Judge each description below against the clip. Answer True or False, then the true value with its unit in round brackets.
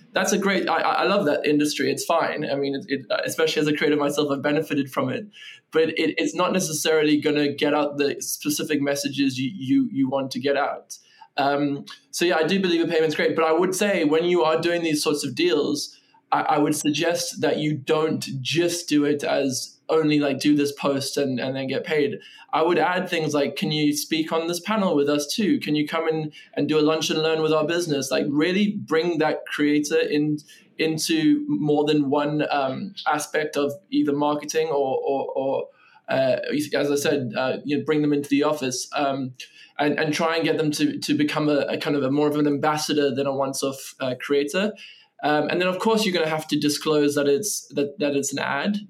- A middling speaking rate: False (225 wpm)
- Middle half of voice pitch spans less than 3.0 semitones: True (2.5 semitones)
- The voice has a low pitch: False (150 Hz)